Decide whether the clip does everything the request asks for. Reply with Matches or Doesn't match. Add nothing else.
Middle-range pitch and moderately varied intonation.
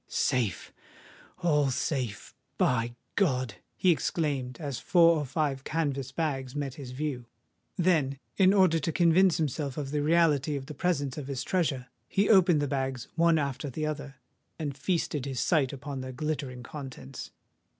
Matches